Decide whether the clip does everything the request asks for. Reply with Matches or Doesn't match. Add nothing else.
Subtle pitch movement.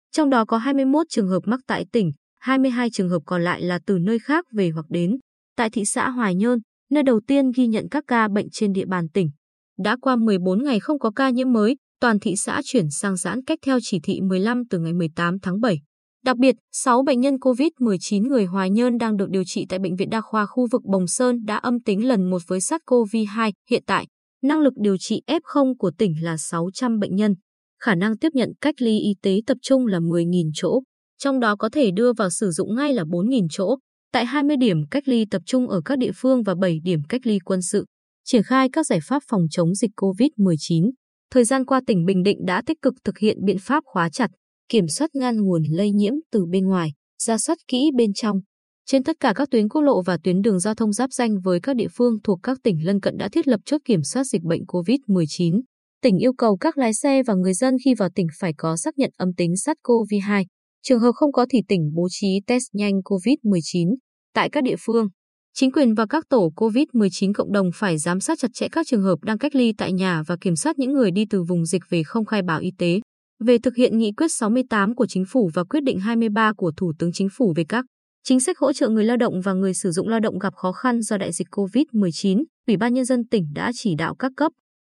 Doesn't match